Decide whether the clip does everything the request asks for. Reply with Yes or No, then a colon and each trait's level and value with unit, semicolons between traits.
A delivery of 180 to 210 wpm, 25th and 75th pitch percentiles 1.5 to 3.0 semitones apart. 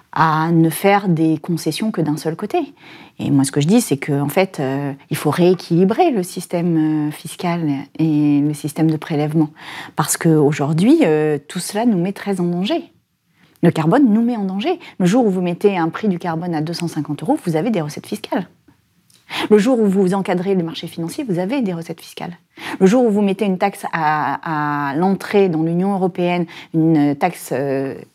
No: average, 195 wpm; average, 3.9 semitones